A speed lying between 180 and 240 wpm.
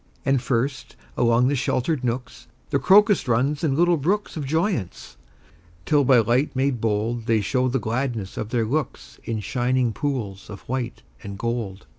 No: average, 165 wpm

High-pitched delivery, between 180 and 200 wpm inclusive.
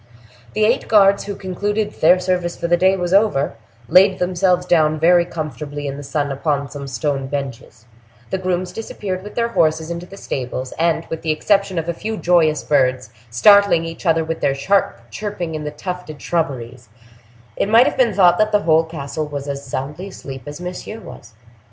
No: medium, 165 Hz; average, 190 wpm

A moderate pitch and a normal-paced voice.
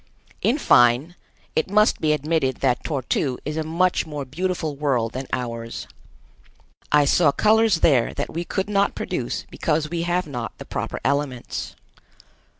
Yes: medium, 150 Hz; average, 155 wpm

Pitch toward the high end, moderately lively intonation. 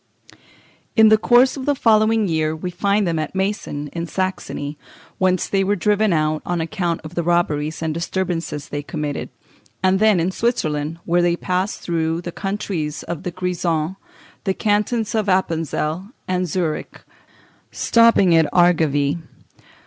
No: medium, 175 Hz; average, 3.7 semitones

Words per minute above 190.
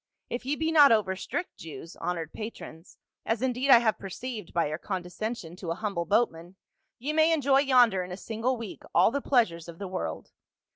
Yes: average, 200 wpm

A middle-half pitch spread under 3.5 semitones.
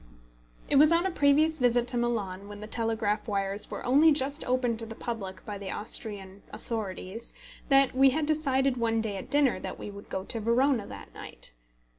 No: average, 4.8 semitones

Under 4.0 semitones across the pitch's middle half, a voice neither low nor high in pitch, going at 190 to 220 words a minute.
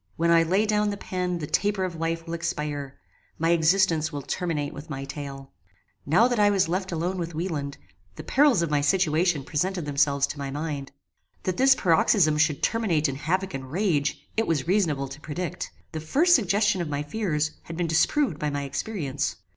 No: average, 4.3 semitones; medium, 165 Hz; average, 195 wpm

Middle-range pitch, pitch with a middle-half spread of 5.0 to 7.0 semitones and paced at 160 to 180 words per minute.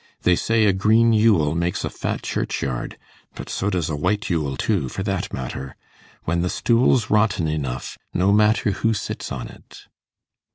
No: very low, 95 Hz; wide, 5.5 semitones; average, 170 wpm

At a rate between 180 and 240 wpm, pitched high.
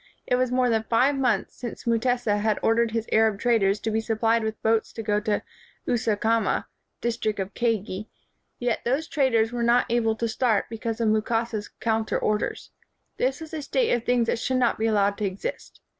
Yes: fast, 205 wpm; high, 225 Hz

